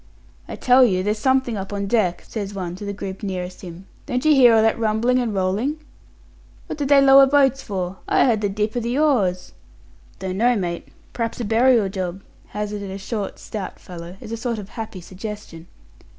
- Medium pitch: No, high, 210 Hz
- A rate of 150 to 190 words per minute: No, average, 200 wpm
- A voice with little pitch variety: No, average, 4.2 semitones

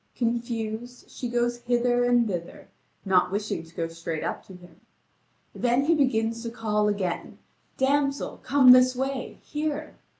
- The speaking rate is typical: Yes, average, 145 wpm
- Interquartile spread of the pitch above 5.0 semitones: No, average, 3.4 semitones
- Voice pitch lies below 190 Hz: No, high, 240 Hz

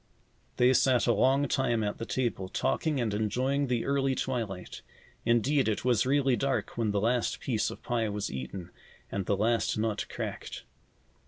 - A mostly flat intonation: No, average, 3.7 semitones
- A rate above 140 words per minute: Yes, average, 170 wpm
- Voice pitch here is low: Yes, low, 120 Hz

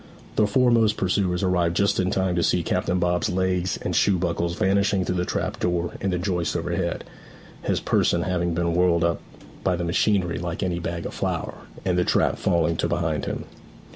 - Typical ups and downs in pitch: No, narrow, 1.6 semitones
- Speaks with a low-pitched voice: Yes, very low, 90 Hz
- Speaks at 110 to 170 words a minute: No, average, 195 wpm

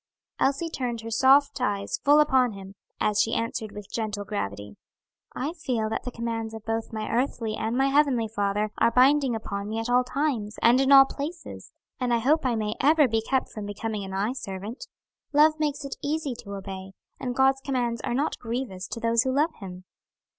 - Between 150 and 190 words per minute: No, average, 200 wpm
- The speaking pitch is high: Yes, high, 235 Hz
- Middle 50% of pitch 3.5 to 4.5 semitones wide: Yes, average, 4.2 semitones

